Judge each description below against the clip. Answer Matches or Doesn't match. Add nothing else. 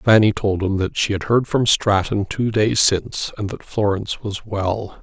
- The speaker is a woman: Doesn't match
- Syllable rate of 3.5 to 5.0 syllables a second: Matches